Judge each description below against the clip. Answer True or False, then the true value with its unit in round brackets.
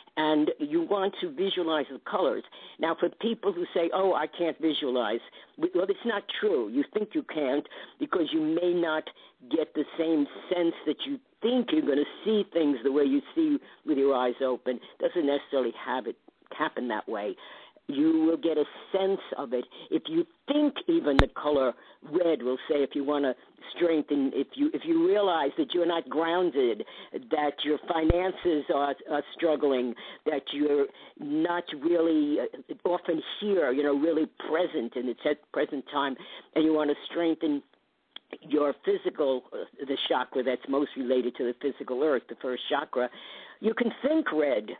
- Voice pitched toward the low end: False (165 Hz)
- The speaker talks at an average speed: True (175 wpm)